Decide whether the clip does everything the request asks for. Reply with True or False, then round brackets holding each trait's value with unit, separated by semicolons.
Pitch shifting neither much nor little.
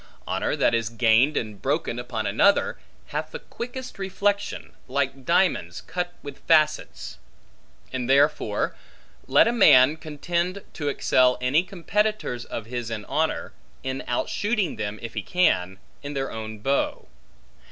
False (7.1 semitones)